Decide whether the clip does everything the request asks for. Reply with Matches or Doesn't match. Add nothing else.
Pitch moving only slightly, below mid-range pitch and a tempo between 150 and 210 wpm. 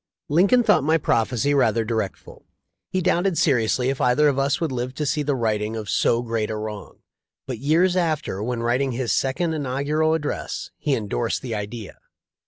Doesn't match